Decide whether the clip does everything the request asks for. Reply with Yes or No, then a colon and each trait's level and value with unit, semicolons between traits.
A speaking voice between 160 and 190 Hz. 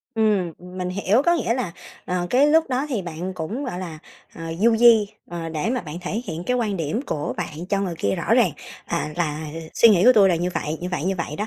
Yes: medium, 185 Hz